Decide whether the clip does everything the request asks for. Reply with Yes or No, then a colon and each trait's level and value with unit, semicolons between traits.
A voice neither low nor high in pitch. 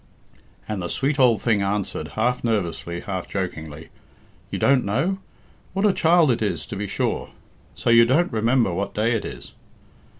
No: low, 110 Hz